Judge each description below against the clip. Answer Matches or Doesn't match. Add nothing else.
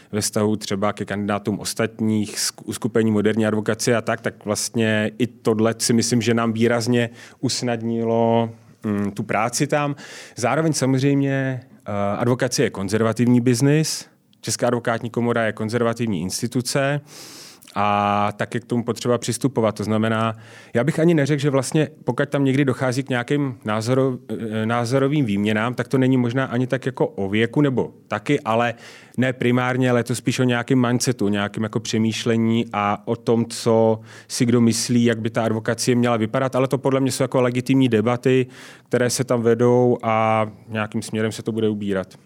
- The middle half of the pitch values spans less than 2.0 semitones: Doesn't match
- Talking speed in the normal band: Matches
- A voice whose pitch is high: Doesn't match